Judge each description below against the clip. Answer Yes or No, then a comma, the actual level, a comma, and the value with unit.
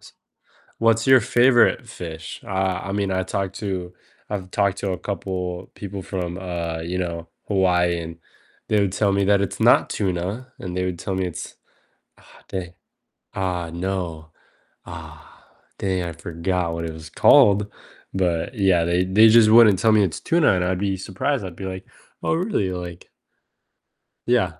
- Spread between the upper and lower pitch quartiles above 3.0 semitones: No, narrow, 2.4 semitones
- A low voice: Yes, very low, 95 Hz